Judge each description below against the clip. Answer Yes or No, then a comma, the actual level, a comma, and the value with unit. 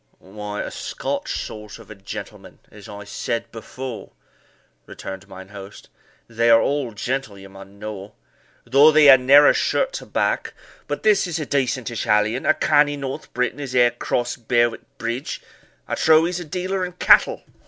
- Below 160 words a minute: No, average, 170 wpm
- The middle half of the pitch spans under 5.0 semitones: No, wide, 5.5 semitones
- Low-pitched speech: Yes, low, 120 Hz